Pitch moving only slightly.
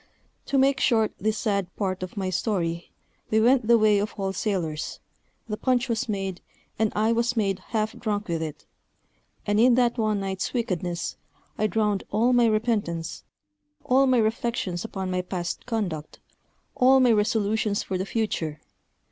No: average, 3.6 semitones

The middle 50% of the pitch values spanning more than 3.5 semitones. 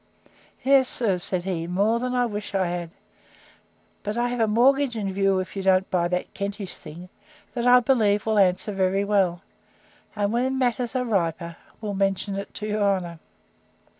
Yes: average, 4.0 semitones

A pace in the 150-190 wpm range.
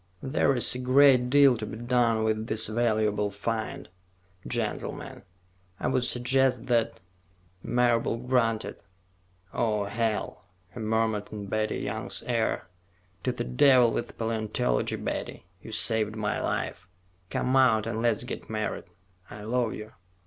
No: average, 140 wpm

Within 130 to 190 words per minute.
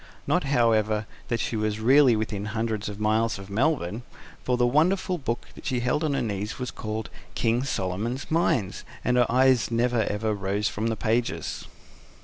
Yes: average, 170 wpm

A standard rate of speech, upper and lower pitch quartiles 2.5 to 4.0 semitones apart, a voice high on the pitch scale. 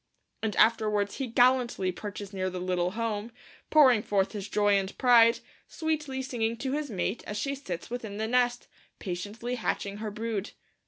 Yes: average, 165 wpm; average, 3.4 semitones; high, 220 Hz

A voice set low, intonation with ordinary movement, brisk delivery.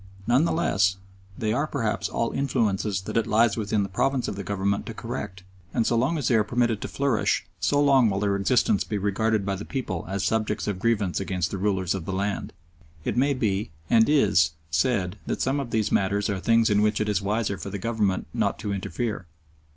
Yes: low, 105 Hz; average, 3.1 semitones; fast, 220 wpm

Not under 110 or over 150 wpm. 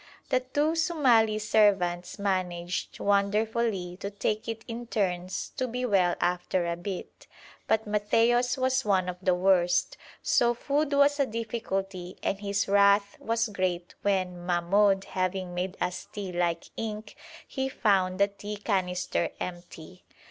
Yes: average, 140 wpm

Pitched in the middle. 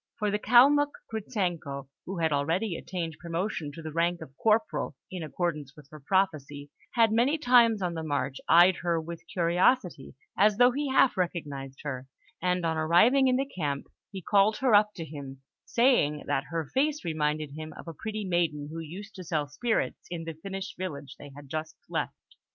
Yes: medium, 170 Hz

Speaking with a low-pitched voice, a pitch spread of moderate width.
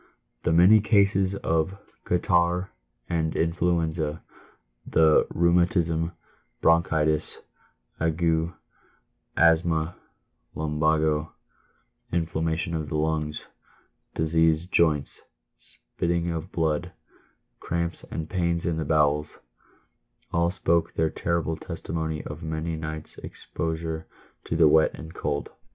No: very low, 80 Hz; narrow, 1.4 semitones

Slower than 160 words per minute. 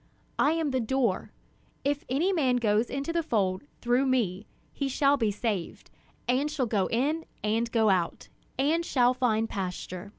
No: average, 165 wpm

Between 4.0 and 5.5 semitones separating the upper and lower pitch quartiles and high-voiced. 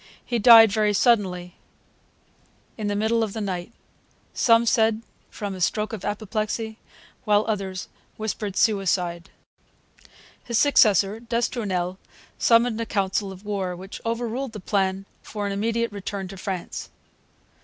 No: average, 2.8 semitones; high, 210 Hz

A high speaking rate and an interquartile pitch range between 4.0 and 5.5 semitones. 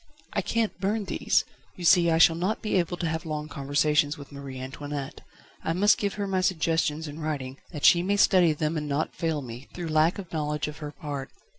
No: fast, 220 wpm; average, 3.4 semitones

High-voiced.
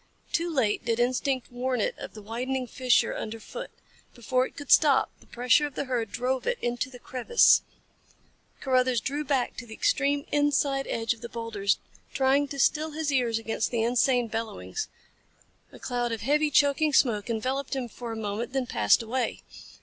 Yes: very high, 255 Hz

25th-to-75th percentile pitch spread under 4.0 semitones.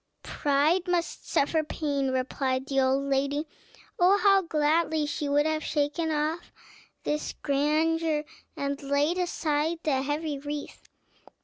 Yes: narrow, 2.4 semitones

